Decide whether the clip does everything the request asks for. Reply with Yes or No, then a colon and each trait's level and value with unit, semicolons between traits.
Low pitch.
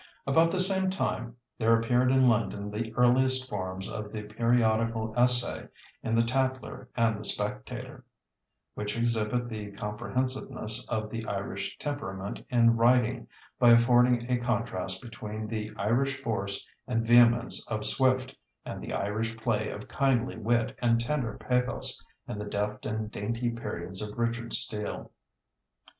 Yes: low, 115 Hz